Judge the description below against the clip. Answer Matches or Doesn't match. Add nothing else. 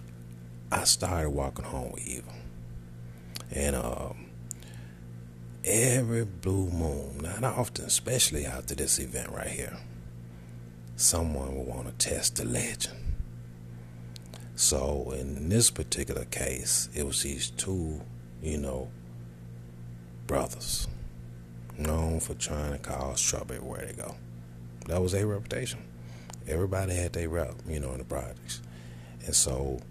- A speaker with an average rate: Doesn't match